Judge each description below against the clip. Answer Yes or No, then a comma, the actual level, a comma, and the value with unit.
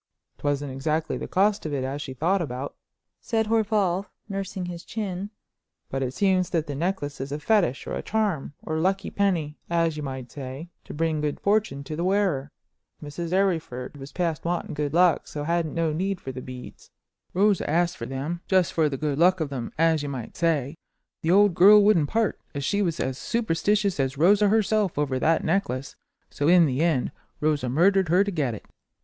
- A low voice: No, medium, 165 Hz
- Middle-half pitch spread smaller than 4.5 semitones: No, average, 5.0 semitones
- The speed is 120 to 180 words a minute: No, average, 200 wpm